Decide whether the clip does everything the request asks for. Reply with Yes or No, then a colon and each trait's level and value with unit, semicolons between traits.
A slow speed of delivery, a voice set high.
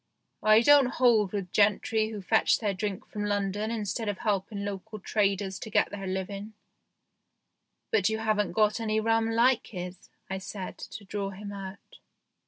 No: average, 170 wpm; high, 205 Hz